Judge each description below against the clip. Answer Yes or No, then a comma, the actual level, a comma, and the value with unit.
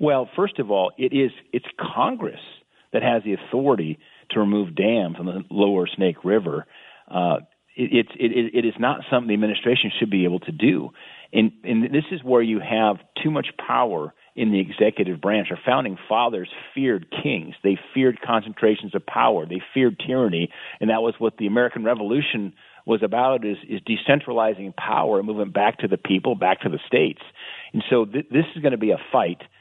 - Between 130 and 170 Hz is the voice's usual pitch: No, low, 110 Hz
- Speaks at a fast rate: No, average, 195 wpm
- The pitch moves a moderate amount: Yes, average, 3.7 semitones